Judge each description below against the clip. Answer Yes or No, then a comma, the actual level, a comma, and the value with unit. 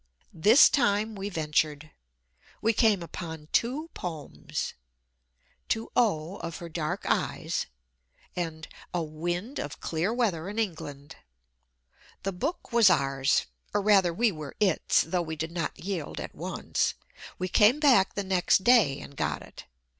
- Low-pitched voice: No, medium, 180 Hz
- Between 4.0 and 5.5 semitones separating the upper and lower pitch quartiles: Yes, average, 5.2 semitones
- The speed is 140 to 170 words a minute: Yes, average, 145 wpm